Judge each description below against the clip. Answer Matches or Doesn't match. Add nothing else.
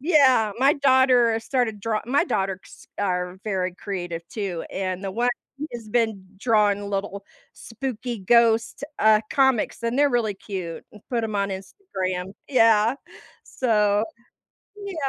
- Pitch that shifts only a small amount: Doesn't match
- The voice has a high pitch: Matches